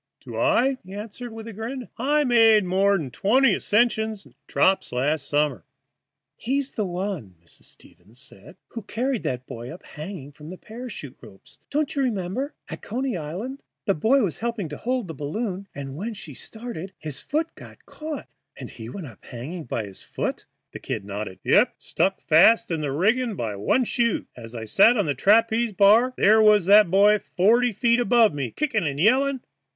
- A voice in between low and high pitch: No, high, 205 Hz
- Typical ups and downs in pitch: No, wide, 7.9 semitones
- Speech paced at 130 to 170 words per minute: No, average, 185 wpm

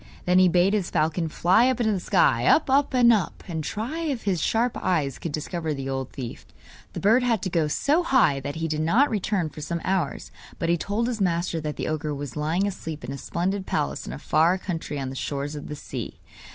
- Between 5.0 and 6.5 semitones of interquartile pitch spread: Yes, wide, 5.5 semitones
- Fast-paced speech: Yes, fast, 235 wpm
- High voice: No, medium, 170 Hz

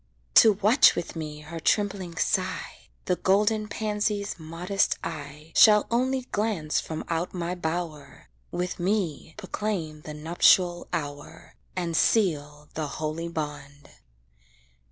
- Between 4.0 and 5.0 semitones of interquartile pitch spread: Yes, average, 4.7 semitones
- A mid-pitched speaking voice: Yes, medium, 170 Hz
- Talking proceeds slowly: Yes, slow, 120 wpm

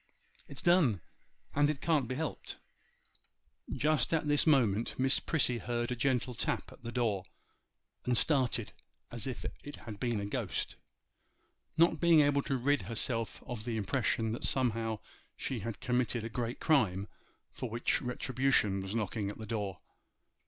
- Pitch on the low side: Yes, low, 120 Hz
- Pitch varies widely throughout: No, average, 3.5 semitones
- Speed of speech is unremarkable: Yes, average, 150 wpm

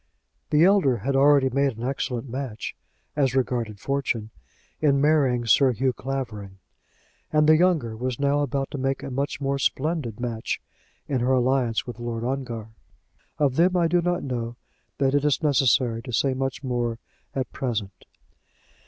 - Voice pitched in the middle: No, low, 130 Hz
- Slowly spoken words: No, average, 160 wpm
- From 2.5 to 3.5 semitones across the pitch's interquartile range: Yes, average, 2.9 semitones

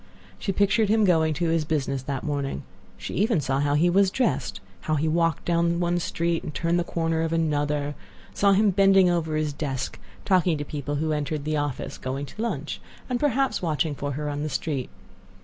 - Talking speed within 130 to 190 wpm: No, fast, 205 wpm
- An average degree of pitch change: Yes, average, 3.4 semitones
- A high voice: No, medium, 160 Hz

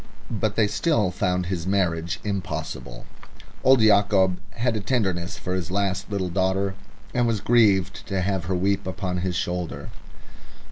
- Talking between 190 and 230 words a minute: No, average, 150 wpm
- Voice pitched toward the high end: No, very low, 95 Hz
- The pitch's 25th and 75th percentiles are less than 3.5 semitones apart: Yes, narrow, 2.4 semitones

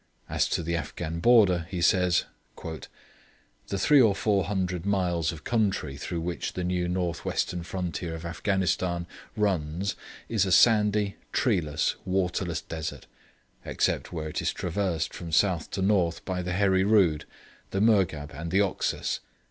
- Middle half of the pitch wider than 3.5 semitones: No, average, 2.9 semitones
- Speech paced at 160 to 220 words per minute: No, average, 150 wpm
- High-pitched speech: No, very low, 90 Hz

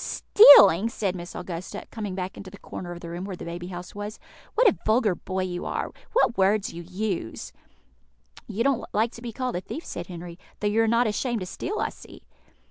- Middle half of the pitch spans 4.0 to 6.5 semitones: Yes, average, 4.3 semitones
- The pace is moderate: No, fast, 215 wpm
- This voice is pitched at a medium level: No, high, 200 Hz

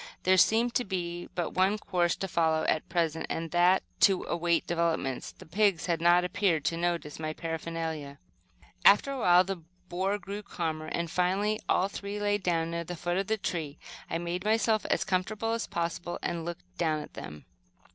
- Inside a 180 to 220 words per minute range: Yes, average, 185 wpm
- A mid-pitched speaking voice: Yes, medium, 175 Hz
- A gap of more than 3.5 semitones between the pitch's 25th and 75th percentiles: No, average, 2.9 semitones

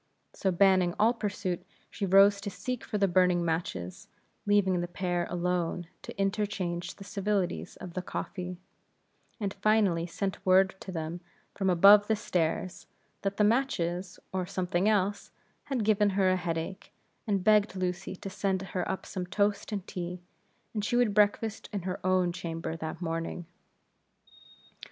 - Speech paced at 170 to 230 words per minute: No, average, 155 wpm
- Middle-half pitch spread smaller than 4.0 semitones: Yes, narrow, 2.5 semitones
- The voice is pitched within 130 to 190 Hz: Yes, medium, 185 Hz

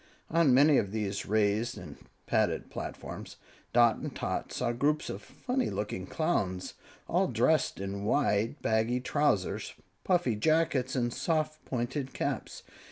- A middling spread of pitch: No, wide, 6.3 semitones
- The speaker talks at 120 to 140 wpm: Yes, slow, 135 wpm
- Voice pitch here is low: Yes, low, 120 Hz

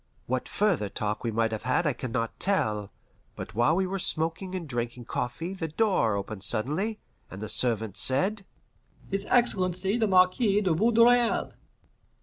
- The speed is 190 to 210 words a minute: No, average, 160 wpm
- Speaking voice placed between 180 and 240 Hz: No, medium, 160 Hz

